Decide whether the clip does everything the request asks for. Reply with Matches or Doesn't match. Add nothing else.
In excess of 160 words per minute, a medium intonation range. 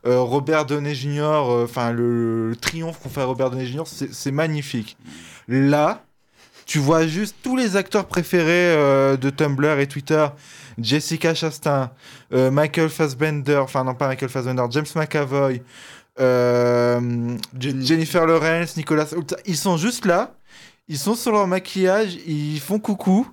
Doesn't match